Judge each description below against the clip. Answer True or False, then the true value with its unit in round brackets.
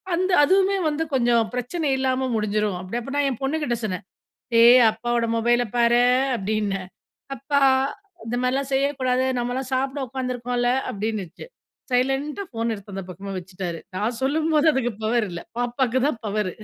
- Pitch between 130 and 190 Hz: False (245 Hz)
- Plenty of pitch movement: False (3.8 semitones)